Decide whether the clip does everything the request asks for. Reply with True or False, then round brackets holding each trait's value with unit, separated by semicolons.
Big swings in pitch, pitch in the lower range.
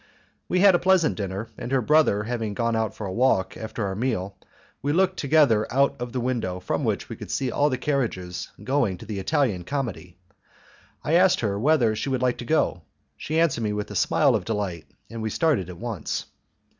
True (5.7 semitones; 120 Hz)